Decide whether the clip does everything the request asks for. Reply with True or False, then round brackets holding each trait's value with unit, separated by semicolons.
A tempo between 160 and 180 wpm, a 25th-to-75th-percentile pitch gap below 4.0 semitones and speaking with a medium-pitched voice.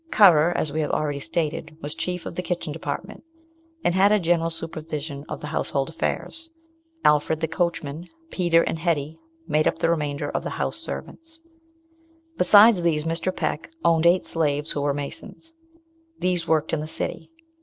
True (170 wpm; 2.6 semitones; 165 Hz)